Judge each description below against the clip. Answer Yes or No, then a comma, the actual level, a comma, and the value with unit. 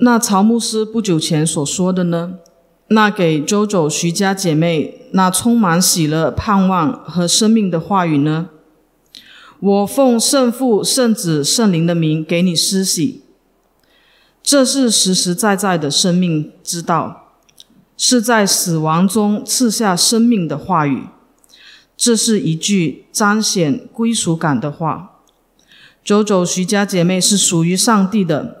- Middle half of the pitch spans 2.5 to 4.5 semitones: No, average, 4.9 semitones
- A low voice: No, high, 190 Hz